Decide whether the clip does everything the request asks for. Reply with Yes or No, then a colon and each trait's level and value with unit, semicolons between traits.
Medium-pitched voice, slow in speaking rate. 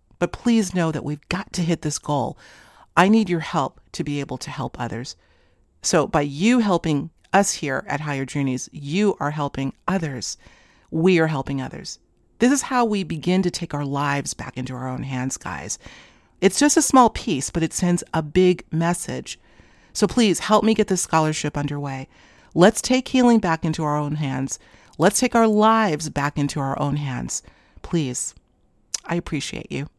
No: medium, 155 Hz; average, 185 wpm